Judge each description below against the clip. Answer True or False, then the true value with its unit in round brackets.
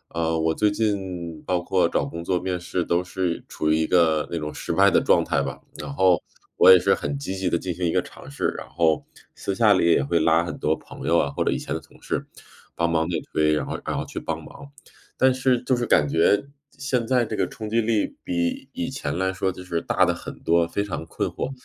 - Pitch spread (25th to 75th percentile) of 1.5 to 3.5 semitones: False (4.3 semitones)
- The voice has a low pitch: True (90 Hz)